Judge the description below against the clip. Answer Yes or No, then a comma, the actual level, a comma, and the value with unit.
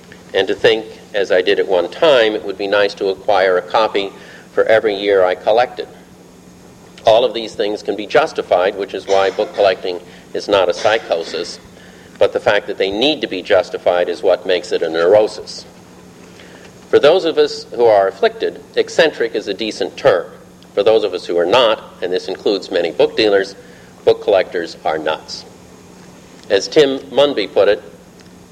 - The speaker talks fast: No, average, 185 wpm